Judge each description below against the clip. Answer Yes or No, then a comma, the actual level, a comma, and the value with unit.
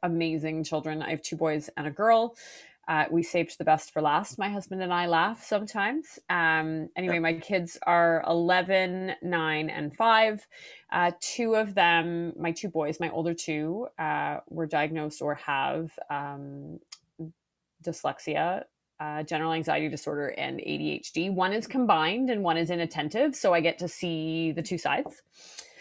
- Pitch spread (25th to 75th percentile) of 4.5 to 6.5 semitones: No, average, 3.2 semitones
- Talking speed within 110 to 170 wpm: Yes, average, 160 wpm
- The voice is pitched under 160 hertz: No, medium, 170 Hz